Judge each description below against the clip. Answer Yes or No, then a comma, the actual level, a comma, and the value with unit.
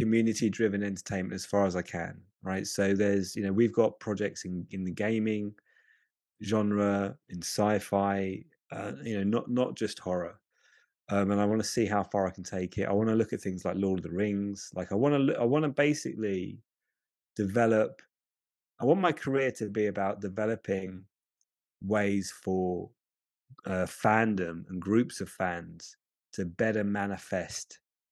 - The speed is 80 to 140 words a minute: No, average, 175 wpm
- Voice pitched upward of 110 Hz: No, low, 100 Hz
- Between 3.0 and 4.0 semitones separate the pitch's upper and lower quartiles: No, narrow, 2.5 semitones